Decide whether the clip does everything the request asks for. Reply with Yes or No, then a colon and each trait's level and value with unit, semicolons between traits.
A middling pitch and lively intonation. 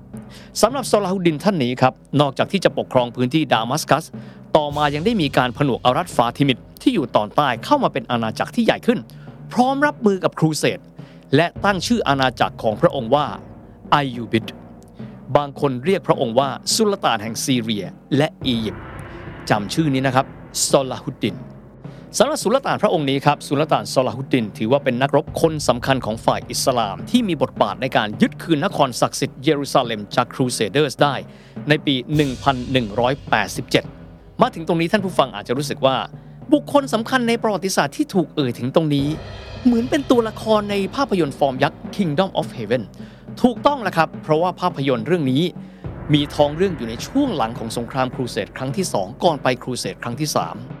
Yes: medium, 145 Hz; wide, 6.6 semitones